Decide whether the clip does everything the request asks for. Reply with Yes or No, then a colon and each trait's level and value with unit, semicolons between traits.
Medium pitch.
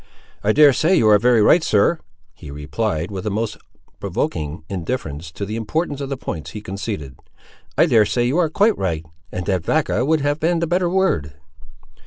No: low, 110 Hz